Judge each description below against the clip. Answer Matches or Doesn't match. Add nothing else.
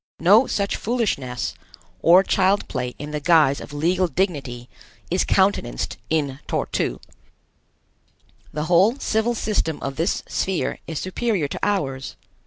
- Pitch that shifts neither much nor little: Doesn't match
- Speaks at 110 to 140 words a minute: Matches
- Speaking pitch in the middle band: Matches